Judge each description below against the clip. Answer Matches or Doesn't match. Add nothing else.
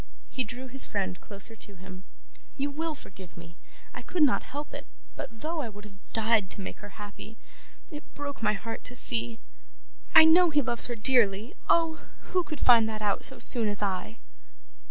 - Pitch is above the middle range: Matches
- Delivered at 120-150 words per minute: Doesn't match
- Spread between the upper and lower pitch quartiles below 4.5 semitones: Doesn't match